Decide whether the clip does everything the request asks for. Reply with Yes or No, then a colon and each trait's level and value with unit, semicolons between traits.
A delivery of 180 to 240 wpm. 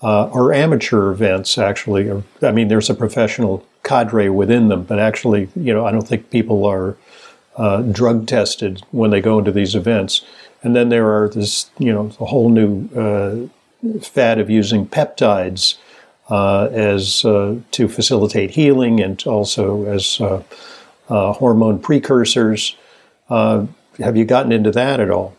No: average, 160 wpm